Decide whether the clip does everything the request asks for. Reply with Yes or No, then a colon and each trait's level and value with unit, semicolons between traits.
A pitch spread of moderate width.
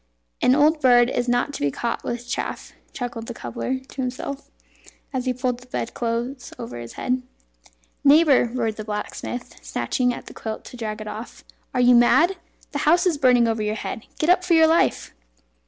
Yes: average, 3.2 semitones